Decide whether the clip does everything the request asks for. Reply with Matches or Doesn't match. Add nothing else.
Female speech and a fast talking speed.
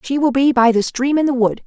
Matches